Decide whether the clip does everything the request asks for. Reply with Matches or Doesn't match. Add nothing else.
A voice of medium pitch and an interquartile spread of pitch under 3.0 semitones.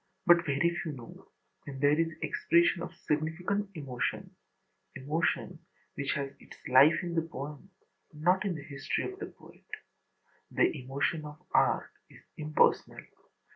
Doesn't match